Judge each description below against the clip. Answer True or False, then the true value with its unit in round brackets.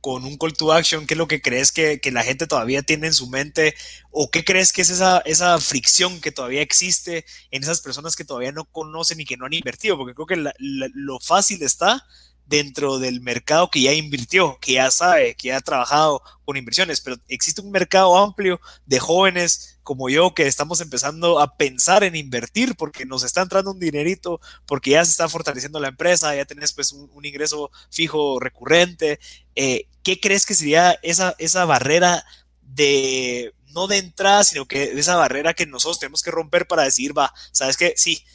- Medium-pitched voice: True (155 Hz)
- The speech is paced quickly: True (200 wpm)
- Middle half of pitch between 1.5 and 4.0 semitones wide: False (4.4 semitones)